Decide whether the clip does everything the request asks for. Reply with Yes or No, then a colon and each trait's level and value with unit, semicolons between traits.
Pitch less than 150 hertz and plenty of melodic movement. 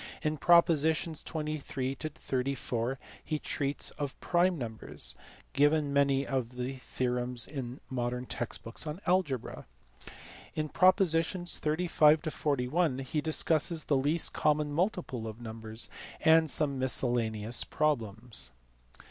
No: medium, 140 Hz; average, 4.1 semitones